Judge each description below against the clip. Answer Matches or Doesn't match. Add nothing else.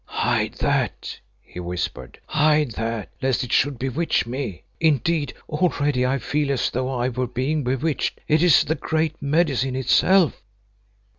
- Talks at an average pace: Matches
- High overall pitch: Doesn't match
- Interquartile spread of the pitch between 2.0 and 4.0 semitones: Matches